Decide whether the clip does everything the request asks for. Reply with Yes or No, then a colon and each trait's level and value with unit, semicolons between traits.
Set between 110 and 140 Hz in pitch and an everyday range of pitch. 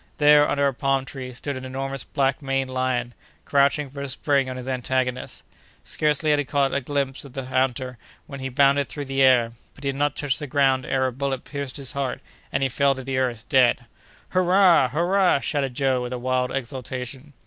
No: low, 135 Hz; narrow, 1.7 semitones